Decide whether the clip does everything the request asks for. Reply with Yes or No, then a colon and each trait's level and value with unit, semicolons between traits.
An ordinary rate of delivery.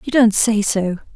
No: fast, 210 wpm